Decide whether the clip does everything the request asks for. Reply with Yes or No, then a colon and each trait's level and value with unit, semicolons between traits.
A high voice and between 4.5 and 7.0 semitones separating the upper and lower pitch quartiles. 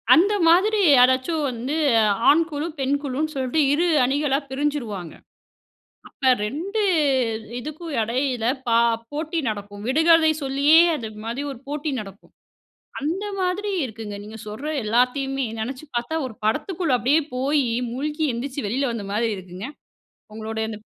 Yes: very high, 270 Hz; average, 5.0 semitones